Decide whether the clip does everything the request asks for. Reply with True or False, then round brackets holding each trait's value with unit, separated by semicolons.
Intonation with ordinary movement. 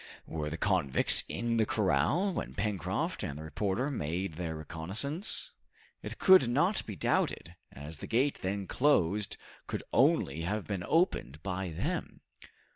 False (6.7 semitones)